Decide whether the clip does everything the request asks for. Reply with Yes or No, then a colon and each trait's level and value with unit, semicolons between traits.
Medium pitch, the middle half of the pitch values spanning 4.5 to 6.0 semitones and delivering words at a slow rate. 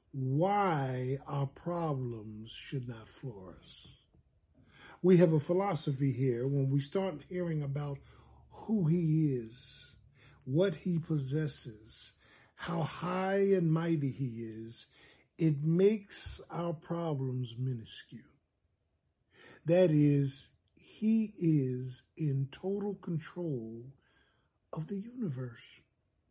Yes: medium, 145 Hz; average, 5.1 semitones; slow, 100 wpm